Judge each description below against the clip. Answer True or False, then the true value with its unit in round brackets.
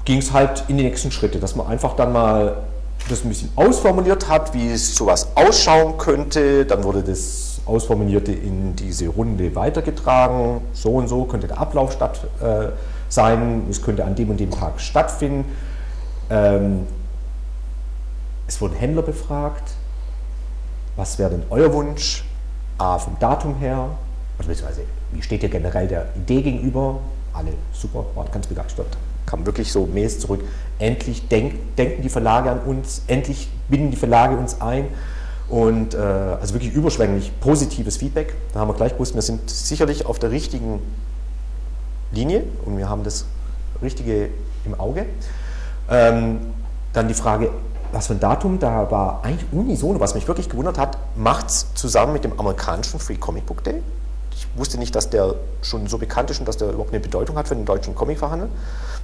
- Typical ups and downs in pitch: False (8.3 semitones)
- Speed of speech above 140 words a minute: True (170 wpm)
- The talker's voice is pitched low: True (110 Hz)